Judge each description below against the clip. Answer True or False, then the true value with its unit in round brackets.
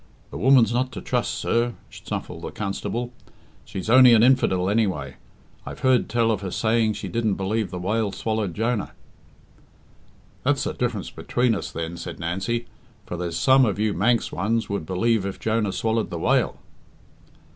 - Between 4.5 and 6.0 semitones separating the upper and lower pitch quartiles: False (3.5 semitones)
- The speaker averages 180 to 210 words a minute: False (170 wpm)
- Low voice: True (110 Hz)